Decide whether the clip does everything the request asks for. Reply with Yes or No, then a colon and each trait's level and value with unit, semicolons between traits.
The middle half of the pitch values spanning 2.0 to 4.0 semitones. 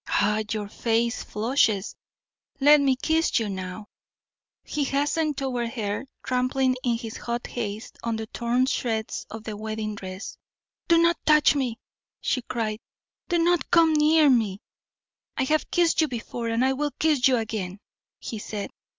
No: average, 4.7 semitones